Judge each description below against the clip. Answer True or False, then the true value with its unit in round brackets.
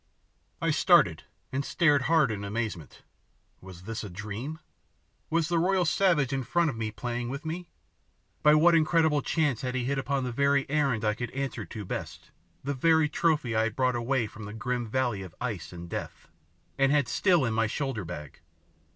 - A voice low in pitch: True (130 Hz)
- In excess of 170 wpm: True (185 wpm)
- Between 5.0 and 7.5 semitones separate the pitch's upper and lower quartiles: True (5.3 semitones)